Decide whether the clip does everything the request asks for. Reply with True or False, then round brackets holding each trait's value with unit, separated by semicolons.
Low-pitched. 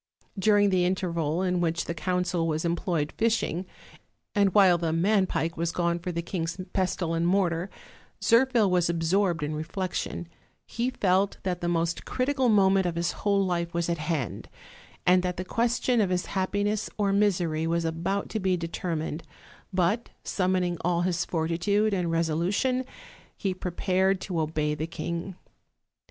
False (180 Hz)